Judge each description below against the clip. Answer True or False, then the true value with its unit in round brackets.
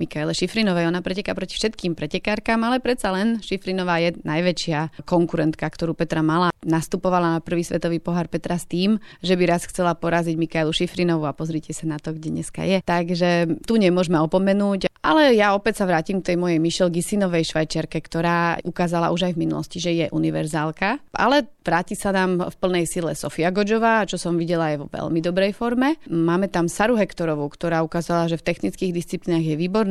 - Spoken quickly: True (185 wpm)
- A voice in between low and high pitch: True (175 Hz)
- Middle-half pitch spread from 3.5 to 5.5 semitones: False (2.6 semitones)